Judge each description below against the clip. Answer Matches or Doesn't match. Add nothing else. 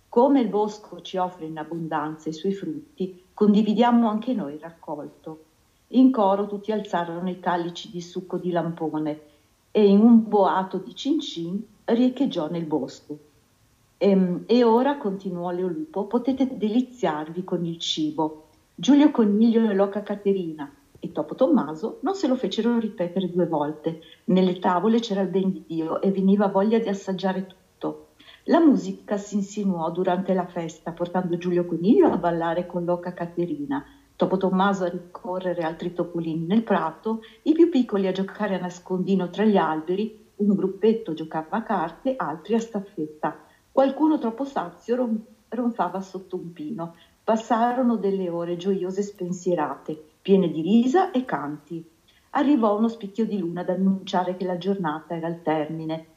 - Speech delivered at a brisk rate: Doesn't match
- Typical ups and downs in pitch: Matches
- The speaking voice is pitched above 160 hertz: Matches